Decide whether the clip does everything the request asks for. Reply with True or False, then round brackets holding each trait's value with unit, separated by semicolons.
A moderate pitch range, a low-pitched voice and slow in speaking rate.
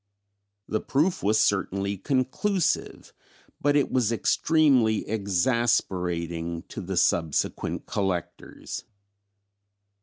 False (6.4 semitones; 105 Hz; 85 wpm)